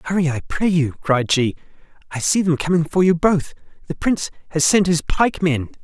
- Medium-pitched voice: Yes, medium, 165 Hz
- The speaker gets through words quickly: No, average, 195 wpm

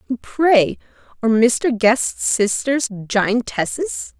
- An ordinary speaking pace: No, slow, 85 wpm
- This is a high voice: Yes, high, 240 Hz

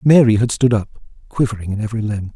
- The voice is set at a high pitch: No, low, 115 Hz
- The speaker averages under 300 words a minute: Yes, fast, 205 wpm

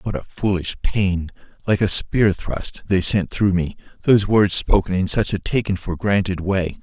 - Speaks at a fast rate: No, average, 185 wpm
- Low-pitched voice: Yes, very low, 95 Hz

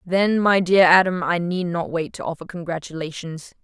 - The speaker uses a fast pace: No, average, 180 wpm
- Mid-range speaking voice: Yes, medium, 175 Hz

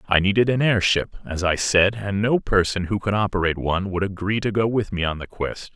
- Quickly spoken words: Yes, fast, 240 wpm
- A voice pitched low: Yes, low, 100 Hz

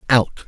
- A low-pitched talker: Yes, low, 120 Hz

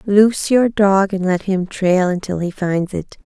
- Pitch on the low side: No, high, 195 Hz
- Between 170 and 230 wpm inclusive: Yes, average, 200 wpm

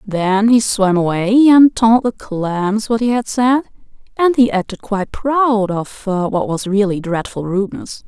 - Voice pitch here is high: Yes, high, 210 Hz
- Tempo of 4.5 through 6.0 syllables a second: No, 4.0 syllables/s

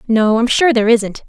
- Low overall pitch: No, high, 230 Hz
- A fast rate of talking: Yes, fast, 235 wpm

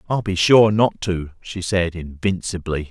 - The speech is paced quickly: No, average, 165 wpm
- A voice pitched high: No, very low, 95 Hz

